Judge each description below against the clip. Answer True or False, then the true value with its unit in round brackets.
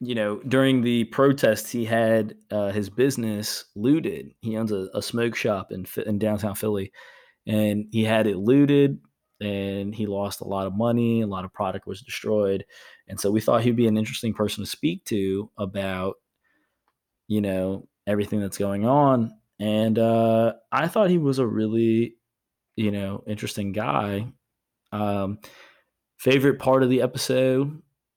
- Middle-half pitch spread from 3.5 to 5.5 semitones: False (2.8 semitones)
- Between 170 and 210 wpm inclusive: False (160 wpm)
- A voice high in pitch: False (110 Hz)